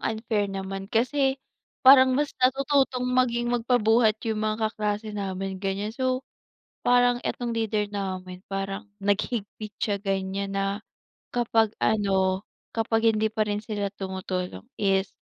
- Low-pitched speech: No, high, 215 Hz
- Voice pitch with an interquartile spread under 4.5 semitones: Yes, average, 3.5 semitones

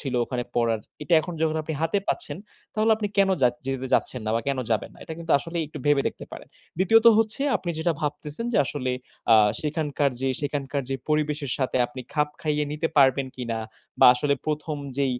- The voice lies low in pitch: No, medium, 150 Hz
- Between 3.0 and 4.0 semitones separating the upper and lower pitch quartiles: Yes, average, 3.5 semitones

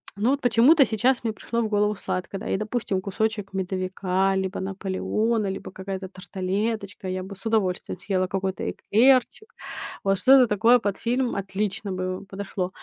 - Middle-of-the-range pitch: No, high, 200 Hz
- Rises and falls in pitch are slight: No, average, 3.0 semitones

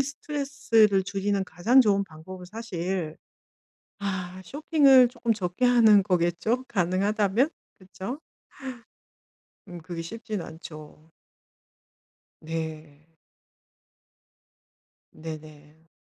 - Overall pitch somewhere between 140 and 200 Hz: Yes, high, 190 Hz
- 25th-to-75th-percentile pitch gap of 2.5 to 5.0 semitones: No, wide, 5.5 semitones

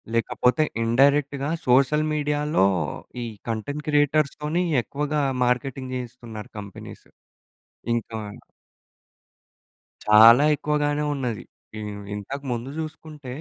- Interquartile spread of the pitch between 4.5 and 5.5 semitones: No, average, 3.8 semitones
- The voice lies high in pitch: No, medium, 140 Hz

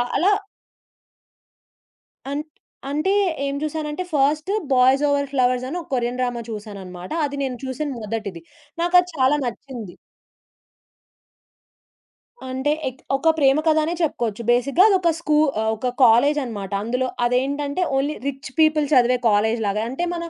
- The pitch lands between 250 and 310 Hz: Yes, very high, 265 Hz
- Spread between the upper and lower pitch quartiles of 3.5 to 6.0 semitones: Yes, average, 4.0 semitones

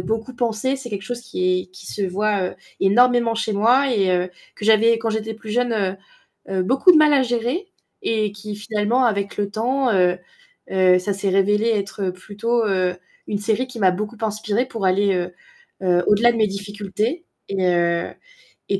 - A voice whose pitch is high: Yes, high, 210 Hz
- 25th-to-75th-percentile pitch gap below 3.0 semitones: No, average, 3.3 semitones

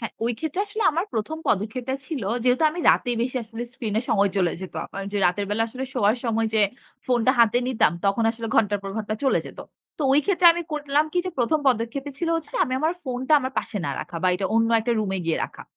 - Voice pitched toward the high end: Yes, high, 240 Hz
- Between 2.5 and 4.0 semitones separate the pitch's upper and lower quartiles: No, average, 4.7 semitones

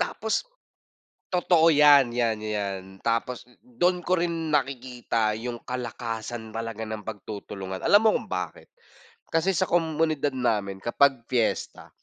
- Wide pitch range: Yes, wide, 6.4 semitones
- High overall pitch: No, low, 125 Hz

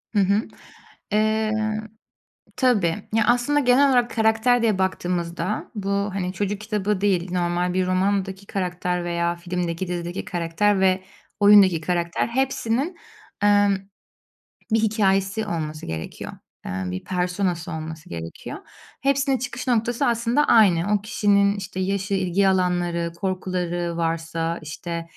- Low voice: No, high, 190 Hz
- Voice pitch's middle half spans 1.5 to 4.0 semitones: Yes, average, 3.7 semitones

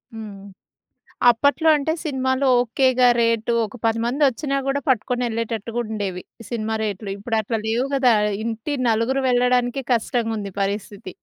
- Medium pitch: No, high, 230 Hz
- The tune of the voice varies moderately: Yes, average, 3.0 semitones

